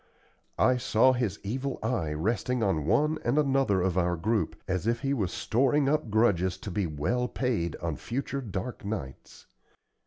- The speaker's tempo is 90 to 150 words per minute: No, average, 165 wpm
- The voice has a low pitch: Yes, low, 110 Hz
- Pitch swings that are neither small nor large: No, wide, 5.7 semitones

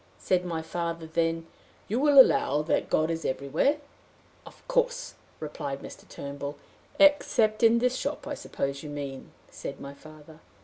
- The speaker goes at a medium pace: Yes, average, 150 wpm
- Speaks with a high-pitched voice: No, medium, 165 Hz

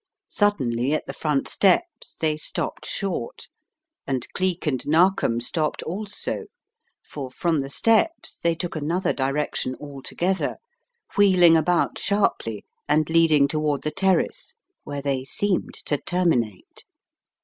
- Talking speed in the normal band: No, slow, 125 wpm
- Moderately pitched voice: Yes, medium, 155 Hz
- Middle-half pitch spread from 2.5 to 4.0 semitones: No, average, 4.9 semitones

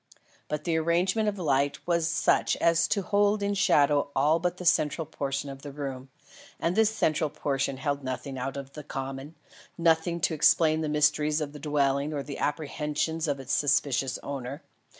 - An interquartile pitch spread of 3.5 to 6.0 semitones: No, average, 3.1 semitones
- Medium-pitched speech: Yes, medium, 150 Hz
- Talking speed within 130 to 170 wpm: No, average, 180 wpm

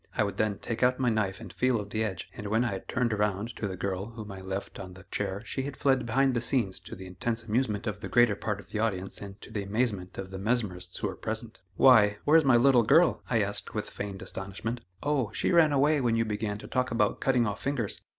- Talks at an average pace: No, fast, 250 wpm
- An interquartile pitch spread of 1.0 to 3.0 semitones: No, average, 3.6 semitones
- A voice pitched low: Yes, low, 110 Hz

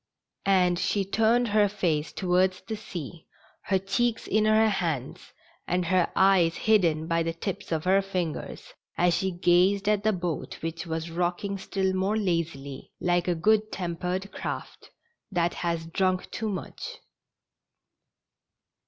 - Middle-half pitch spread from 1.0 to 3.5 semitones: Yes, average, 2.8 semitones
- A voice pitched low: No, medium, 185 Hz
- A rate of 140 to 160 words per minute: Yes, average, 145 wpm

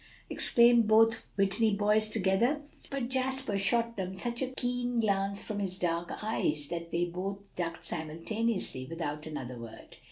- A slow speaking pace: No, average, 155 wpm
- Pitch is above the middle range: Yes, high, 200 Hz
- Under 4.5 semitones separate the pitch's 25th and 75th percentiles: No, wide, 5.4 semitones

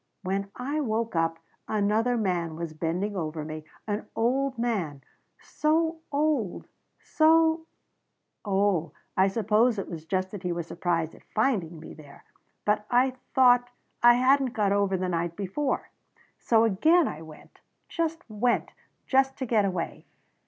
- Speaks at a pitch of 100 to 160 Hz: No, high, 210 Hz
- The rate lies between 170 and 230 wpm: No, average, 145 wpm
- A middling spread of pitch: No, wide, 6.5 semitones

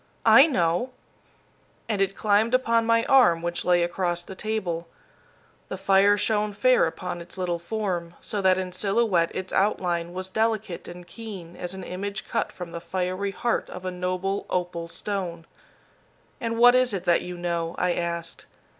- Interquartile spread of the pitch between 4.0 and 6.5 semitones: No, average, 3.3 semitones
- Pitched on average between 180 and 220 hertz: Yes, medium, 185 Hz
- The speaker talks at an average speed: Yes, average, 170 wpm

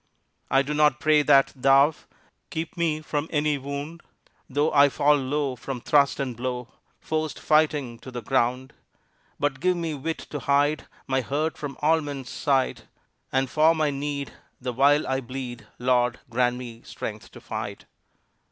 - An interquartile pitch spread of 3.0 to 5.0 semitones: No, narrow, 2.6 semitones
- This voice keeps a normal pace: Yes, average, 160 wpm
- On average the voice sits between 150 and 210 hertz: No, medium, 140 Hz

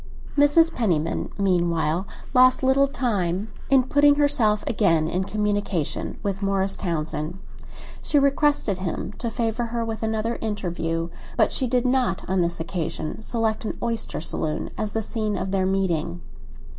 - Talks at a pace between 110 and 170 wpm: Yes, average, 145 wpm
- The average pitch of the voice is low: No, high, 210 Hz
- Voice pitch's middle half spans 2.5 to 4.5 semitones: No, average, 5.3 semitones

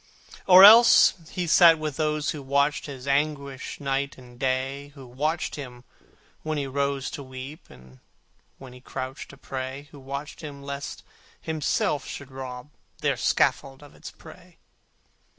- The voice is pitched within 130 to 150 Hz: Yes, medium, 140 Hz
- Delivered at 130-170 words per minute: Yes, average, 150 wpm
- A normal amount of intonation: No, narrow, 2.2 semitones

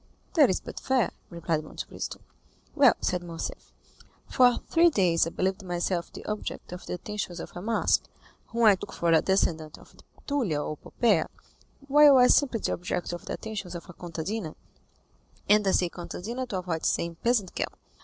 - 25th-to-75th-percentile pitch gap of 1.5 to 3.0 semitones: No, average, 5.2 semitones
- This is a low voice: No, medium, 185 Hz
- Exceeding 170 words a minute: Yes, average, 185 wpm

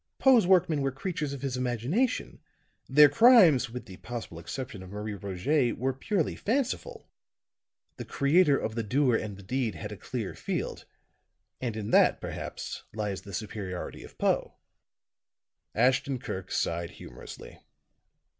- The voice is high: No, low, 125 Hz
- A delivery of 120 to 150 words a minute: Yes, average, 145 wpm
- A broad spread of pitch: Yes, wide, 6.2 semitones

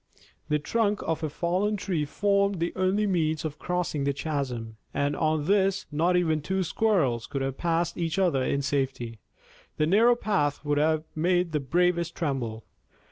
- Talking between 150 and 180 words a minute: Yes, average, 170 wpm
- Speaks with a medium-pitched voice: Yes, medium, 160 Hz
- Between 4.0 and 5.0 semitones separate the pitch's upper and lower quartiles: Yes, average, 4.4 semitones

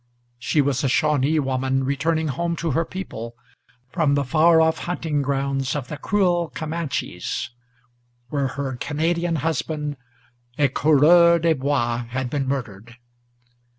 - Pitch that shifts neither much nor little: Yes, average, 3.4 semitones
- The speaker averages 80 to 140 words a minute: Yes, slow, 135 wpm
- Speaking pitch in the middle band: Yes, medium, 145 Hz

